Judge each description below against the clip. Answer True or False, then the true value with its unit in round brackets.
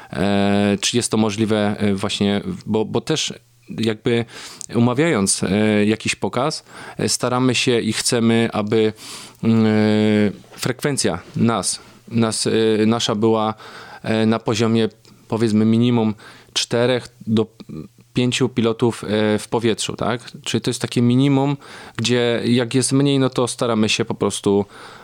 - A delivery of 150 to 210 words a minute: False (115 wpm)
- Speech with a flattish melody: True (2.2 semitones)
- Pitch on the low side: True (115 Hz)